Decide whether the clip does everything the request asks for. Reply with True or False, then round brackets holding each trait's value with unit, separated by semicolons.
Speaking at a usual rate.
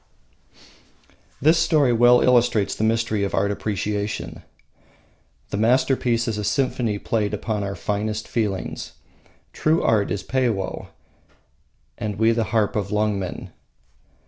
False (120 wpm)